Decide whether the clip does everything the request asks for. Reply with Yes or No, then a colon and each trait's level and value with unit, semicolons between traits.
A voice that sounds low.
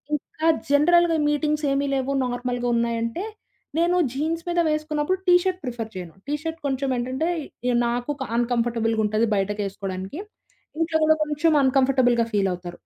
No: very high, 260 Hz